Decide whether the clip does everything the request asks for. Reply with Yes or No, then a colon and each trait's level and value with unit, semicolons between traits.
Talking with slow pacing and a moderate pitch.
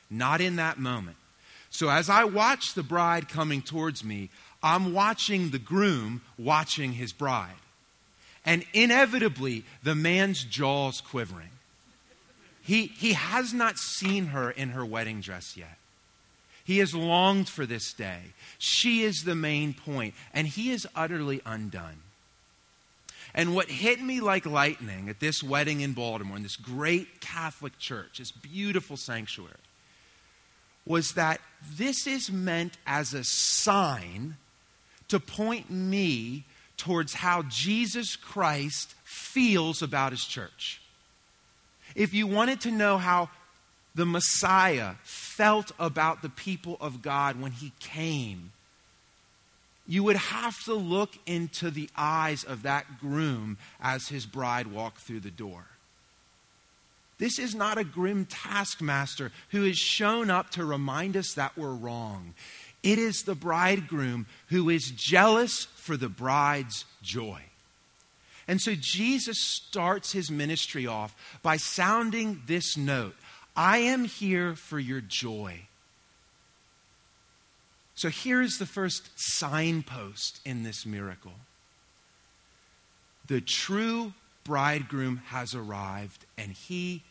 Yes: slow, 125 wpm; medium, 155 Hz